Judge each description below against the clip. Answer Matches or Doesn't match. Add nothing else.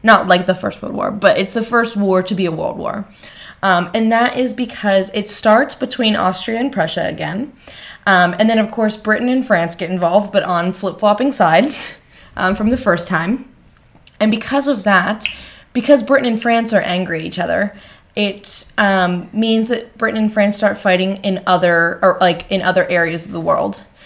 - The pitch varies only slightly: Doesn't match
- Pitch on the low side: Doesn't match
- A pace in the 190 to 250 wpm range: Matches